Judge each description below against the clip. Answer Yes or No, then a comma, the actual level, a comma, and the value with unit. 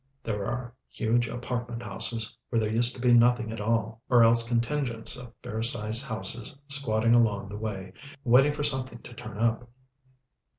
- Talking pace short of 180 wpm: Yes, average, 170 wpm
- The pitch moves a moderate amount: No, narrow, 1.7 semitones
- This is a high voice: No, low, 115 Hz